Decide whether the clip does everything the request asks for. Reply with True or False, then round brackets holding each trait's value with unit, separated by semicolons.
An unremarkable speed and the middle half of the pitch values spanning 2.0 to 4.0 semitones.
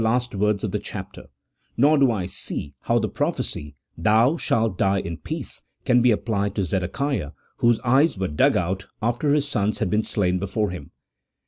False (185 wpm; 4.4 semitones)